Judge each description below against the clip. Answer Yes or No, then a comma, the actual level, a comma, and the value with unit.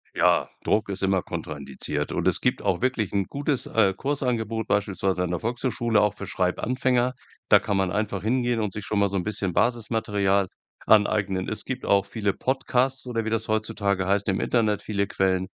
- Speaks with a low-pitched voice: Yes, low, 105 Hz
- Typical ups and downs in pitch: Yes, average, 3.3 semitones